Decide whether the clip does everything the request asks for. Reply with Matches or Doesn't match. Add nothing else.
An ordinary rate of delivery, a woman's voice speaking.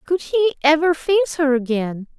Matches